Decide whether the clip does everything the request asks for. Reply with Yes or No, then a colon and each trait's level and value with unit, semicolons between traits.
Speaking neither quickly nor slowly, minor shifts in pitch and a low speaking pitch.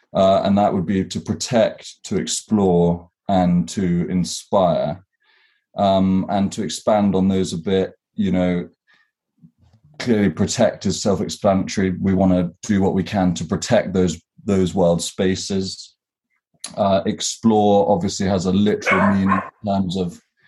Yes: average, 145 wpm; narrow, 1.9 semitones; very low, 95 Hz